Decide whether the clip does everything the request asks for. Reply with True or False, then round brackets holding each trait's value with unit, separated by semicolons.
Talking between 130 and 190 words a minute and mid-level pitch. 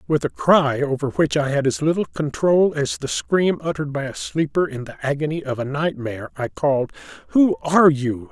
False (200 wpm; 150 Hz)